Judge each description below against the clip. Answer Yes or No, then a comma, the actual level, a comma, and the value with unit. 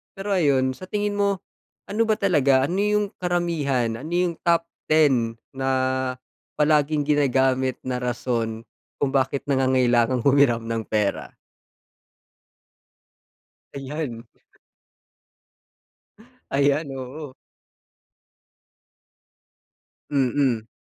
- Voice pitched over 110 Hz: Yes, medium, 140 Hz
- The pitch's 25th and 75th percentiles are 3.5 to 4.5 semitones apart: Yes, average, 4.2 semitones